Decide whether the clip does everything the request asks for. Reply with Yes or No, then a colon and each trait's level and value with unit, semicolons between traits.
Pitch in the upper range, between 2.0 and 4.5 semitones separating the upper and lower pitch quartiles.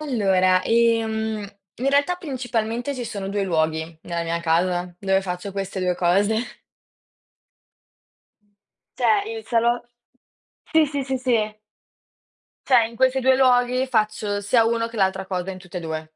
No: high, 215 Hz; average, 5.0 semitones